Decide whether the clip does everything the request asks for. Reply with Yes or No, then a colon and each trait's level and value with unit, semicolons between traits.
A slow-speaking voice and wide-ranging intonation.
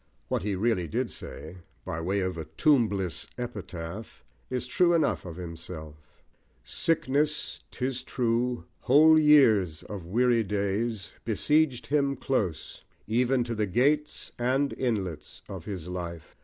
Yes: slow, 130 wpm; wide, 6.3 semitones